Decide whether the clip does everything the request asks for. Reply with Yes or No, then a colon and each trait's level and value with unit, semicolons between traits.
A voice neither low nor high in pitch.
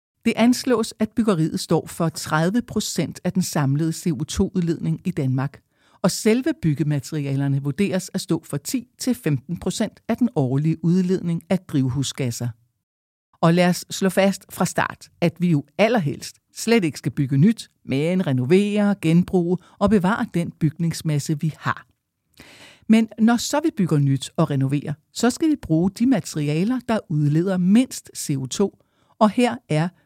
Yes: medium, 170 Hz